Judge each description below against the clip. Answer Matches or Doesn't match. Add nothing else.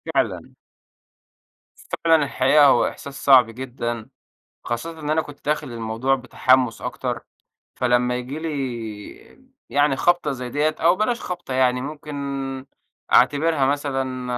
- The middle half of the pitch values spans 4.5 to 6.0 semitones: Doesn't match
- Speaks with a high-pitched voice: Doesn't match